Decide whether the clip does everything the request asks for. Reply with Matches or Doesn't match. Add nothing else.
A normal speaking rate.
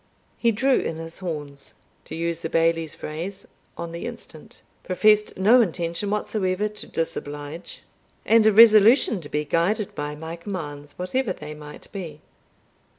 Matches